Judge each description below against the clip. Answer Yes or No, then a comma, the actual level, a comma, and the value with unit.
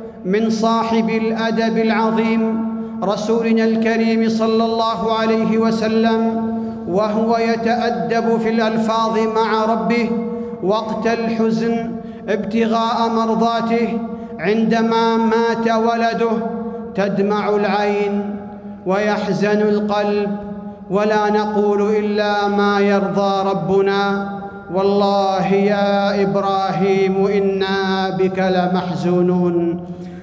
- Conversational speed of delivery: Yes, average, 75 wpm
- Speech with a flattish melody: Yes, narrow, 2.2 semitones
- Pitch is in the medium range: No, high, 220 Hz